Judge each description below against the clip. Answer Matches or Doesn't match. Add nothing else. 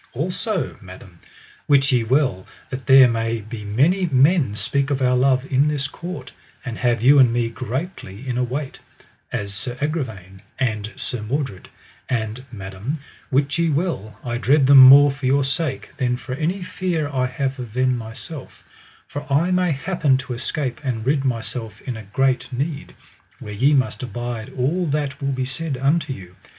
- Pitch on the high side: Doesn't match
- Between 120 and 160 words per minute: Doesn't match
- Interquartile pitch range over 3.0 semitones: Matches